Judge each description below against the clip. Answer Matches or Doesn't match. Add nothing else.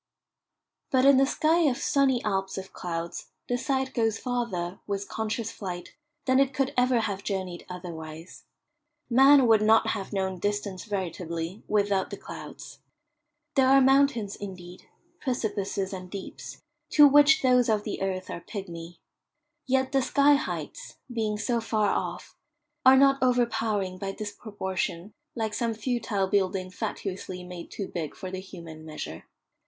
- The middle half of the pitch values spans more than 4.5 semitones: Matches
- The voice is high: Matches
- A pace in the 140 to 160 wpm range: Matches